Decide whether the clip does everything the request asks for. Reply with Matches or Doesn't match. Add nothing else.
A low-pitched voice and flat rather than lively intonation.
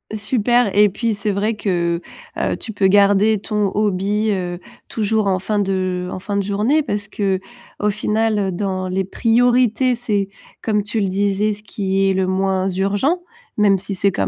Doesn't match